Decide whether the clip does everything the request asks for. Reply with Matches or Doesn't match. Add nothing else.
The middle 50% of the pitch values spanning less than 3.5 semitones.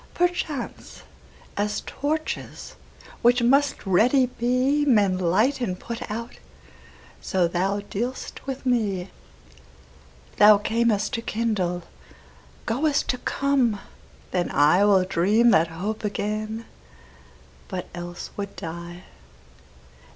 Doesn't match